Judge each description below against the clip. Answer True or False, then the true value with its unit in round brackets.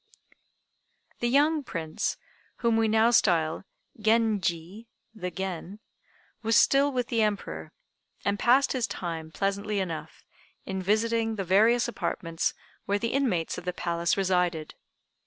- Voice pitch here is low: False (200 Hz)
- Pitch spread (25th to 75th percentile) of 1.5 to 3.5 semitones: False (4.8 semitones)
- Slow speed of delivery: True (130 wpm)